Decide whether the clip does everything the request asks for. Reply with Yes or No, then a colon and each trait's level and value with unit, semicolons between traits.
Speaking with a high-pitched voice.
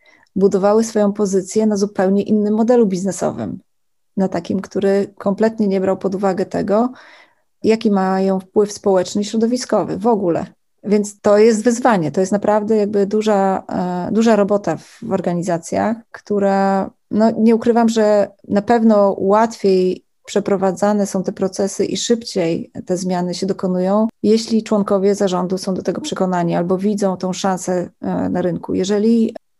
Yes: high, 200 Hz